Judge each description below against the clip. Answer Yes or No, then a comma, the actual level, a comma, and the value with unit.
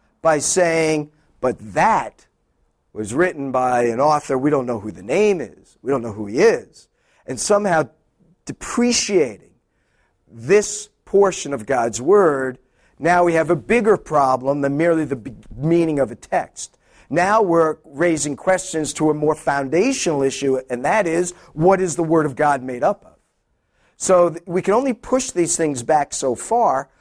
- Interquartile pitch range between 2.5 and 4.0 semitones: No, average, 4.6 semitones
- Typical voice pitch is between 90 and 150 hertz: No, medium, 160 Hz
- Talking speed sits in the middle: Yes, average, 170 wpm